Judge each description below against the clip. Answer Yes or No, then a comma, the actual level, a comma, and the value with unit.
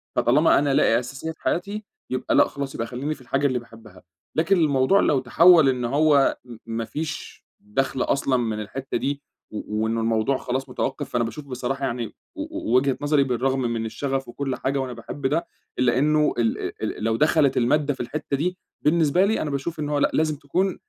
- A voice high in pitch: No, low, 135 Hz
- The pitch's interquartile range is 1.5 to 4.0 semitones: Yes, average, 3.6 semitones